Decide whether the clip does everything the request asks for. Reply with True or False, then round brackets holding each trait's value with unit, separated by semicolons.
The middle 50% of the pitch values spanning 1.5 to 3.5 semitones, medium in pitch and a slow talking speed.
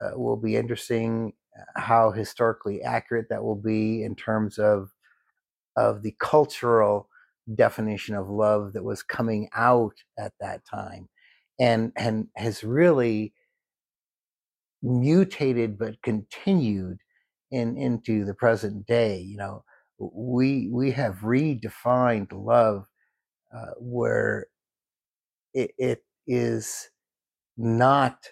False (2.4 semitones; 115 Hz; 110 wpm)